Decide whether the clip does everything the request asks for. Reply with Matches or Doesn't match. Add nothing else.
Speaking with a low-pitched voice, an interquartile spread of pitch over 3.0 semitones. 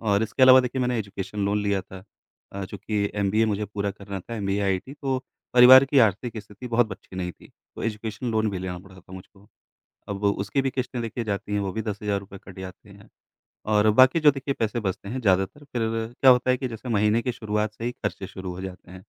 Matches